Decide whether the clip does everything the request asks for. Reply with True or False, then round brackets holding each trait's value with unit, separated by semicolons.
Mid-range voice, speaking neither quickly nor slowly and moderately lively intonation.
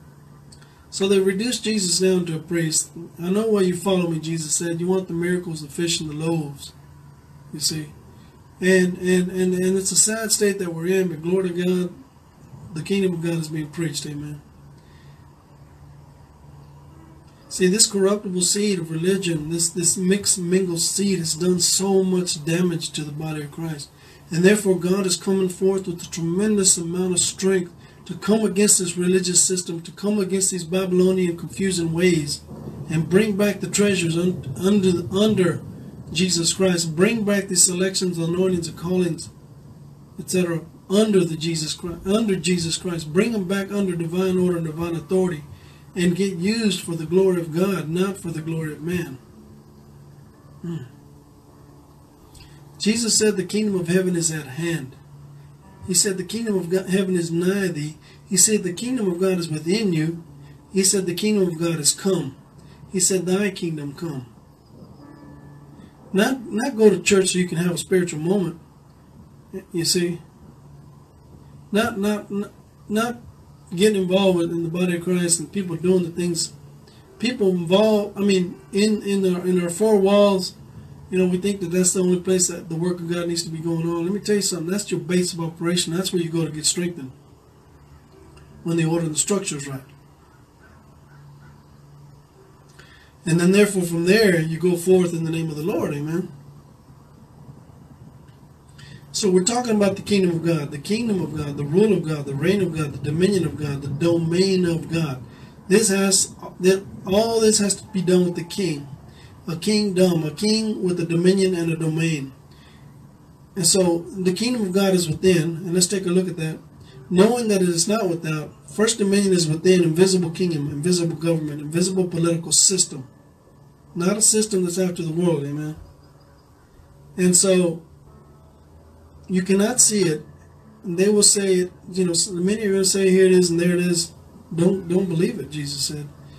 True (175 Hz; 180 wpm; 3.2 semitones)